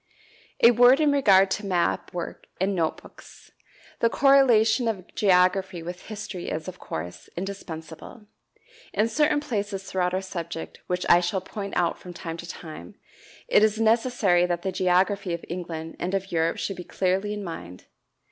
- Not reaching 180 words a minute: Yes, average, 165 wpm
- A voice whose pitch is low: No, high, 190 Hz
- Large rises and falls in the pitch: No, average, 3.4 semitones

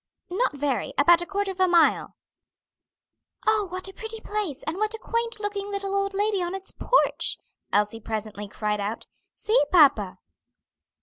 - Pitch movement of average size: No, wide, 6.9 semitones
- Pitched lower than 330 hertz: No, very high, 375 Hz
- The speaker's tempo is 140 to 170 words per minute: Yes, average, 165 wpm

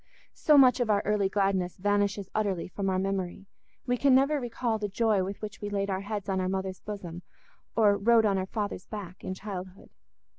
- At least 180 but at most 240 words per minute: Yes, average, 200 wpm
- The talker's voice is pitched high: Yes, high, 200 Hz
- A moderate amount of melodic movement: No, narrow, 2.2 semitones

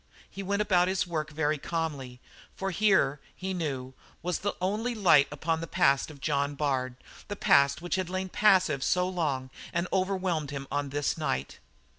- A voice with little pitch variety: No, average, 4.8 semitones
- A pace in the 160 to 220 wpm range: Yes, average, 175 wpm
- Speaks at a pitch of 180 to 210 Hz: No, medium, 165 Hz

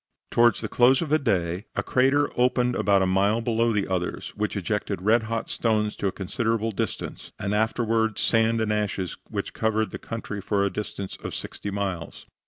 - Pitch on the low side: Yes, low, 110 Hz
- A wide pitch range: No, narrow, 2.6 semitones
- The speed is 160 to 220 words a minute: Yes, average, 190 wpm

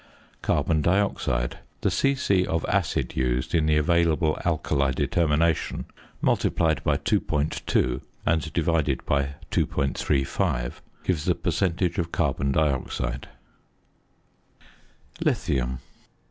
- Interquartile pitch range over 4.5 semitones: No, average, 3.6 semitones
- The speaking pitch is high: No, very low, 75 Hz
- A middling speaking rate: No, slow, 95 wpm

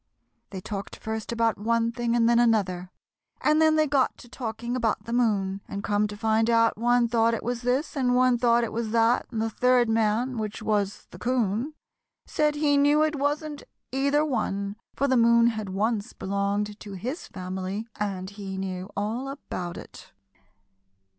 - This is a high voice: Yes, high, 230 Hz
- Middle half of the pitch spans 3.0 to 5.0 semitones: Yes, average, 3.4 semitones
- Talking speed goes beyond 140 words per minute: Yes, average, 180 wpm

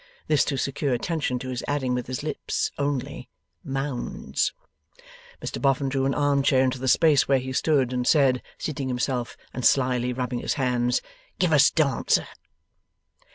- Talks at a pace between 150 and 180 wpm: Yes, average, 160 wpm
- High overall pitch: No, low, 130 Hz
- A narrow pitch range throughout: Yes, narrow, 2.2 semitones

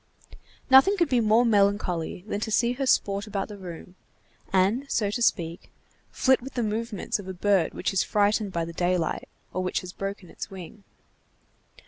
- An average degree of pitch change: Yes, average, 3.9 semitones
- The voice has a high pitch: Yes, high, 205 Hz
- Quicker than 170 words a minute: Yes, average, 180 wpm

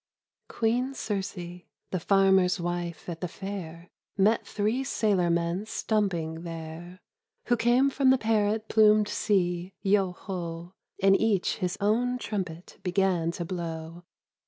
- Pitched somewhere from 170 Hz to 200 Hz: Yes, high, 190 Hz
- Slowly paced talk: Yes, slow, 130 wpm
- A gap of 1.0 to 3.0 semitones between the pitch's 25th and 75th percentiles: No, average, 3.6 semitones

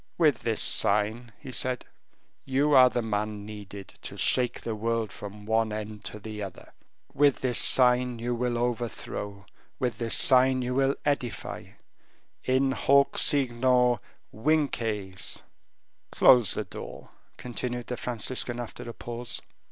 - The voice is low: Yes, low, 120 Hz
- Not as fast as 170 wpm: Yes, slow, 135 wpm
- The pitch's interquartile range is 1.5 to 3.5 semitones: Yes, average, 3.0 semitones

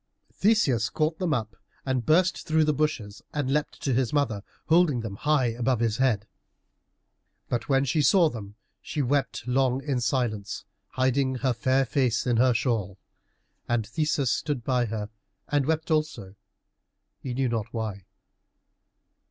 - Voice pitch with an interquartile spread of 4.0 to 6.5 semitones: Yes, average, 4.3 semitones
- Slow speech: No, average, 150 wpm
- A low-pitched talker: Yes, low, 130 Hz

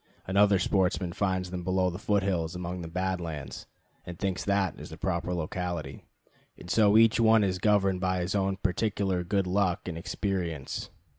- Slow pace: No, average, 175 wpm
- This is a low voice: Yes, very low, 95 Hz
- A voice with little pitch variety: Yes, narrow, 2.0 semitones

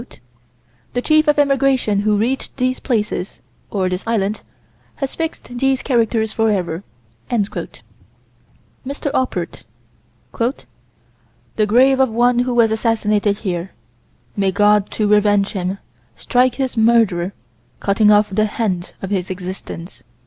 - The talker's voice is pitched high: Yes, high, 215 Hz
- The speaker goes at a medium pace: No, slow, 125 wpm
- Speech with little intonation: No, average, 3.9 semitones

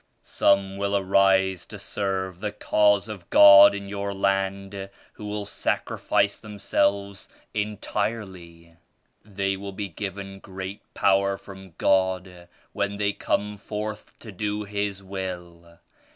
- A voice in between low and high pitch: No, low, 100 Hz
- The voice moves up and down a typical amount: No, narrow, 1.2 semitones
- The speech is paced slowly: Yes, slow, 125 wpm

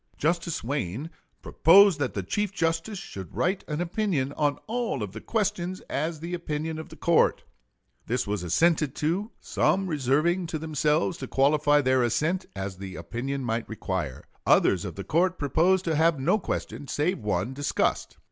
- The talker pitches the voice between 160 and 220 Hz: No, medium, 150 Hz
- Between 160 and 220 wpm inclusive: Yes, average, 165 wpm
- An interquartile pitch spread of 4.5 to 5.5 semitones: Yes, average, 5.0 semitones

